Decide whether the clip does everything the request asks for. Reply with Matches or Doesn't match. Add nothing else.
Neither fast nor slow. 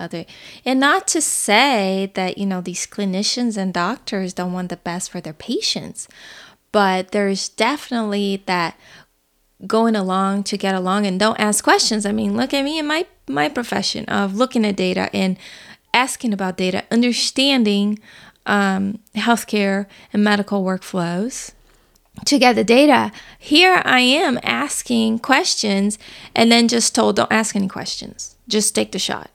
Matches